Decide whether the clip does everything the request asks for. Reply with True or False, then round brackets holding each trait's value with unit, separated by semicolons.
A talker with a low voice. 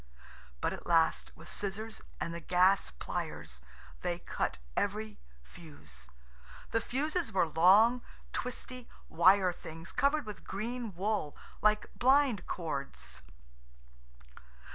False (195 Hz)